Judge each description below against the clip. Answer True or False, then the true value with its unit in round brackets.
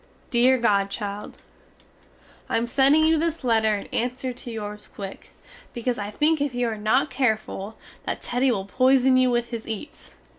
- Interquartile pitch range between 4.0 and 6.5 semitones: False (3.3 semitones)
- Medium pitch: False (240 Hz)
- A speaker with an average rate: True (170 wpm)